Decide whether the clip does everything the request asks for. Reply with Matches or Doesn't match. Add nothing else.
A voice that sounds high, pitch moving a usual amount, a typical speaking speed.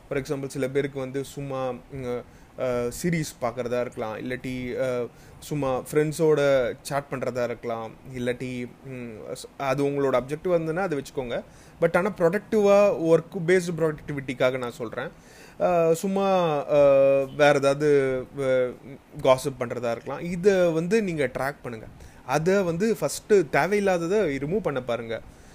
Doesn't match